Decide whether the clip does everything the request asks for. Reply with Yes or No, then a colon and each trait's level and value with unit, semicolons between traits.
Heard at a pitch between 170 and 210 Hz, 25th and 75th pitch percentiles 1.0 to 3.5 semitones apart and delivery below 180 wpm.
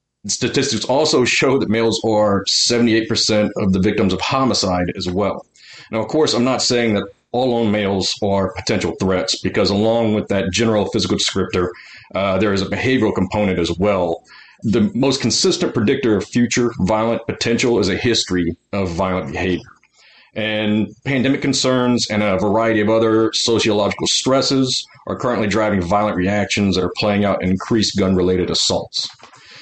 No: low, 105 Hz; average, 3.2 semitones; average, 160 wpm